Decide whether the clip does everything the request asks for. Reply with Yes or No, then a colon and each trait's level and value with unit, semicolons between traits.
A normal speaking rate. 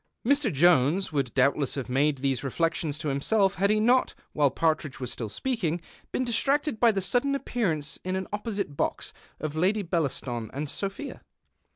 Yes: average, 170 wpm